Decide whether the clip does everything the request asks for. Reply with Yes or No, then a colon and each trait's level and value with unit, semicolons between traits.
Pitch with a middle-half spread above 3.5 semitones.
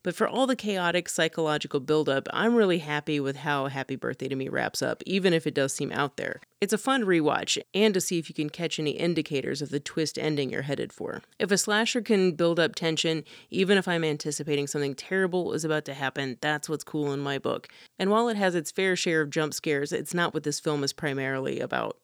Yes: average, 4.1 semitones